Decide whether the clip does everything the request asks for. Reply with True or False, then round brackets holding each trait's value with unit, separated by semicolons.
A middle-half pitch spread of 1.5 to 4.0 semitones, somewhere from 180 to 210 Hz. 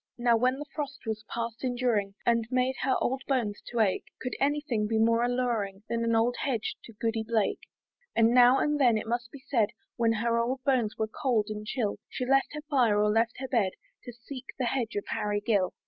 False (2.5 semitones; 235 Hz)